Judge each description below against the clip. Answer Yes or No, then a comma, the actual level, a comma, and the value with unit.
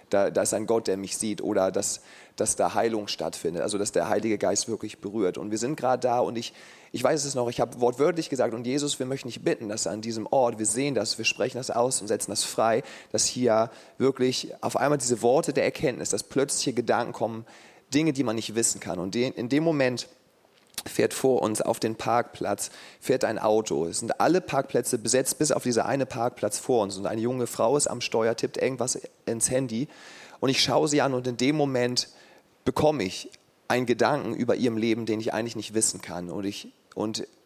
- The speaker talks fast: Yes, fast, 220 wpm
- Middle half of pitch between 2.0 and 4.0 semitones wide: Yes, average, 2.8 semitones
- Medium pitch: No, low, 120 Hz